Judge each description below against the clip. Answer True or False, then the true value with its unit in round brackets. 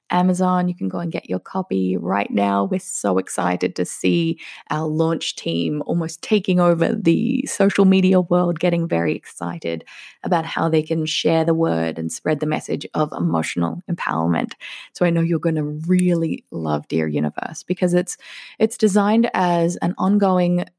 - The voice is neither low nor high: True (165 Hz)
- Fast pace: False (170 wpm)